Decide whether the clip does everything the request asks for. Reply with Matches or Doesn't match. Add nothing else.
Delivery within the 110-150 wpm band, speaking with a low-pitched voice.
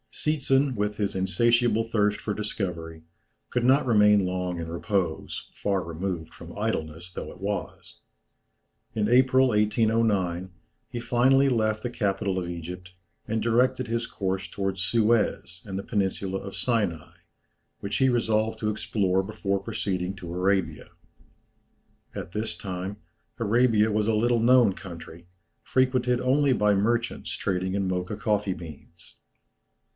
Matches